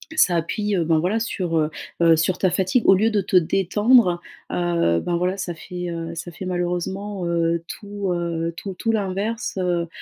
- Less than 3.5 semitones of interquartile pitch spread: Yes, average, 2.8 semitones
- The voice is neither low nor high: Yes, medium, 180 Hz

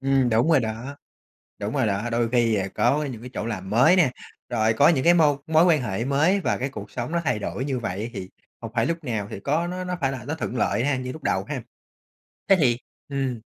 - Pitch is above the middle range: No, low, 130 Hz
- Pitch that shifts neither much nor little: Yes, average, 4.9 semitones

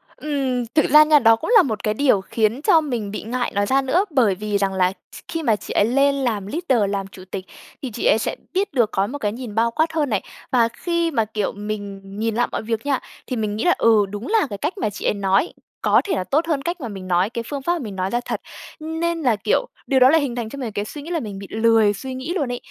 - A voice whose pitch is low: No, high, 240 Hz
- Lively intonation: Yes, wide, 5.8 semitones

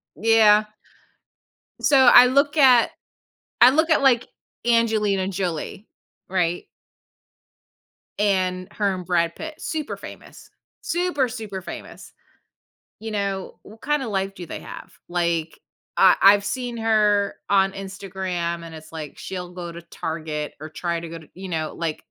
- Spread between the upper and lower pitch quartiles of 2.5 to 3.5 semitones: No, average, 4.7 semitones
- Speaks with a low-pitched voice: No, high, 195 Hz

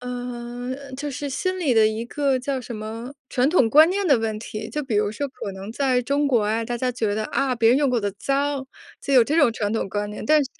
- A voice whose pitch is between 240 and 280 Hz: Yes, very high, 250 Hz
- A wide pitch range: No, average, 4.0 semitones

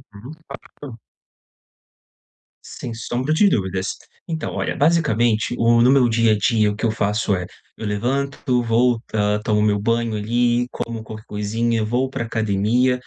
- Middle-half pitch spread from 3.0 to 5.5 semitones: No, narrow, 2.6 semitones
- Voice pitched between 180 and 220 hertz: No, low, 115 Hz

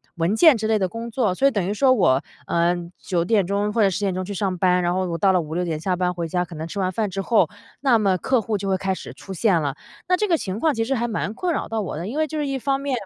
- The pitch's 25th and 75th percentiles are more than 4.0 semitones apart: Yes, average, 4.4 semitones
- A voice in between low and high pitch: No, high, 200 Hz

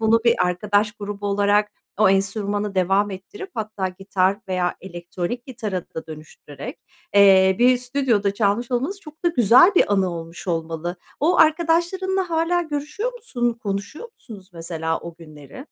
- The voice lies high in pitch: Yes, high, 205 Hz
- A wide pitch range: Yes, wide, 5.9 semitones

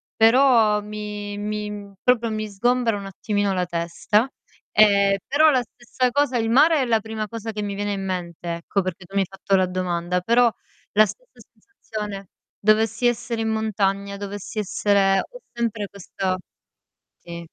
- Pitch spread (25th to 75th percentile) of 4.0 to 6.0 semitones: No, average, 2.7 semitones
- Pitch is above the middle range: Yes, high, 210 Hz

